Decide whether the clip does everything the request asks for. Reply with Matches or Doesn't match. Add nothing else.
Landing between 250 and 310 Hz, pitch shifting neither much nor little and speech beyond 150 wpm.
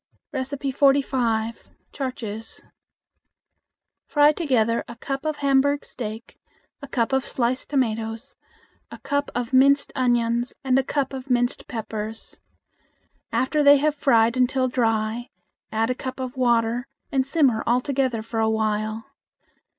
Doesn't match